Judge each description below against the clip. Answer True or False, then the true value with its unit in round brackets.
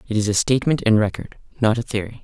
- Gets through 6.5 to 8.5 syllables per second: True (7.0 syllables/s)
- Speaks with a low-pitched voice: True (110 Hz)